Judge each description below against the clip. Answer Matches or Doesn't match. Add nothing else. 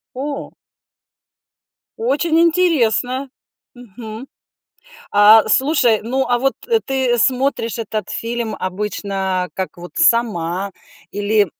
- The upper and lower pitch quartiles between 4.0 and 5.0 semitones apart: Matches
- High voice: Matches